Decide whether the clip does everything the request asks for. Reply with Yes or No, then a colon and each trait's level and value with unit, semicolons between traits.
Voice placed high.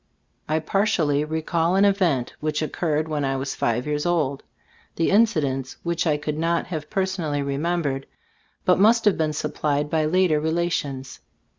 No: medium, 155 Hz